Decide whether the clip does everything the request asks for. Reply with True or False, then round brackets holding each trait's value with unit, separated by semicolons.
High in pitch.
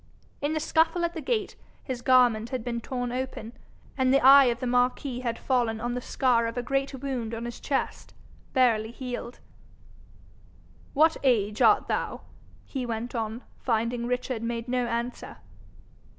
True (245 Hz)